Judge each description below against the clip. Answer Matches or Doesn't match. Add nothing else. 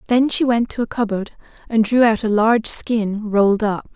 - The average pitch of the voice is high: Matches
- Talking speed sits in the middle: Doesn't match